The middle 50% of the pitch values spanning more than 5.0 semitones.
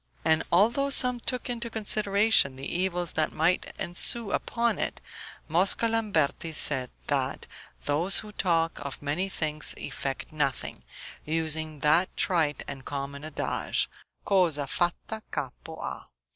Yes: wide, 5.6 semitones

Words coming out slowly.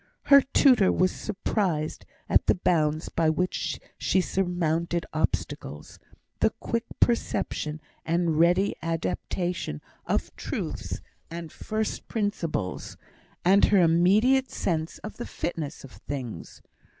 Yes: slow, 115 wpm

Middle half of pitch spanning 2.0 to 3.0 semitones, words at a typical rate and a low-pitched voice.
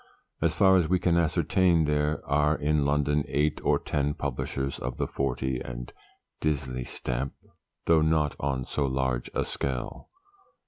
Yes: average, 2.7 semitones; average, 150 wpm; very low, 75 Hz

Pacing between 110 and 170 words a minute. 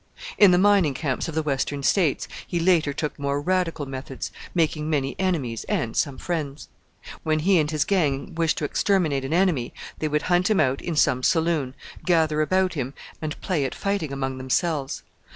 No: average, 185 wpm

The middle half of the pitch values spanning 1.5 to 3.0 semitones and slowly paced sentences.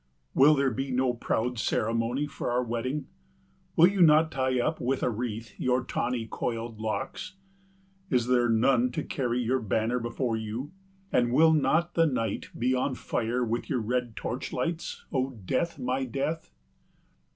No: narrow, 2.6 semitones; average, 160 wpm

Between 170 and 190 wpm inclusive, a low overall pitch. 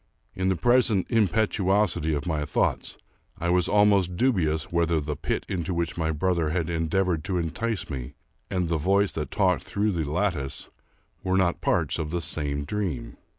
Yes: average, 175 wpm; very low, 85 Hz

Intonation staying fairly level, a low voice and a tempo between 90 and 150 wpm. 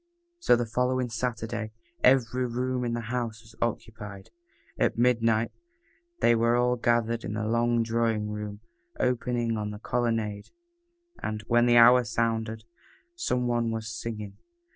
Yes: narrow, 1.6 semitones; low, 115 Hz; average, 140 wpm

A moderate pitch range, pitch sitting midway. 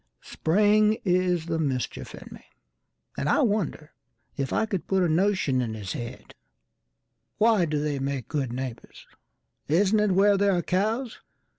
No: wide, 6.8 semitones; medium, 175 Hz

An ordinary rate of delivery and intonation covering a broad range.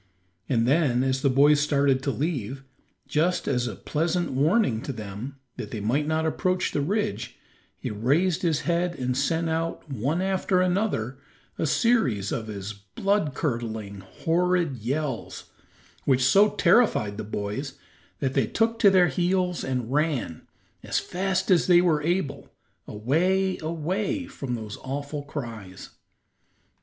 Yes: average, 145 wpm; wide, 6.4 semitones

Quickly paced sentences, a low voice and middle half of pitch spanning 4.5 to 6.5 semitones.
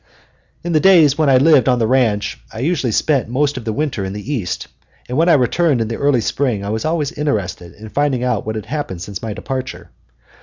Yes: fast, 230 wpm; low, 130 Hz; average, 5.2 semitones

